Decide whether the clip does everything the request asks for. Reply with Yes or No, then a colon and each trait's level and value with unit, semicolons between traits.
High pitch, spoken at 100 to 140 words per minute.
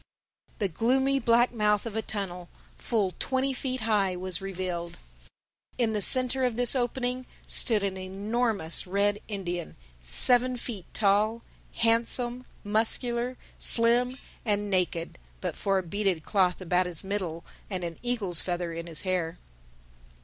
Yes: high, 205 Hz; slow, 135 wpm